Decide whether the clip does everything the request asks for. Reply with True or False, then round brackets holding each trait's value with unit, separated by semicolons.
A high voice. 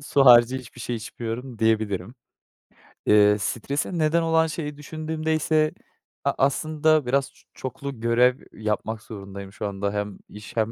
False (125 Hz)